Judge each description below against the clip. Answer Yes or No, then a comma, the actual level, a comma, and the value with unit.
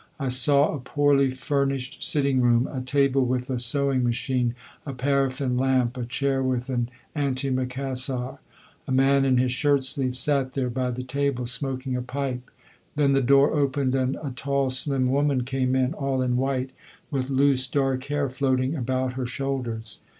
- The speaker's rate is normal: Yes, average, 170 wpm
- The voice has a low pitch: Yes, low, 130 Hz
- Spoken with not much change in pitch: Yes, narrow, 1.4 semitones